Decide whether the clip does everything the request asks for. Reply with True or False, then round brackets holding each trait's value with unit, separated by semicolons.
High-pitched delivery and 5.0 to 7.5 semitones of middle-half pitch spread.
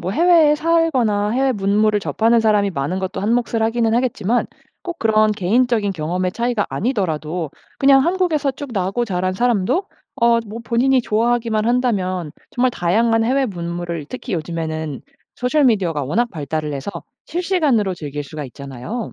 True (215 Hz; 5.5 semitones)